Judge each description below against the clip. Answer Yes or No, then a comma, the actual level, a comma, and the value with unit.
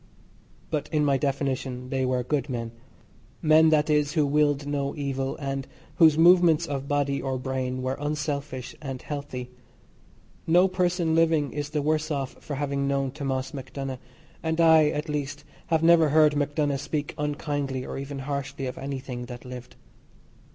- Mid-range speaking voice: Yes, medium, 145 Hz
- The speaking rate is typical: Yes, average, 160 wpm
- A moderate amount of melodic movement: No, narrow, 2.2 semitones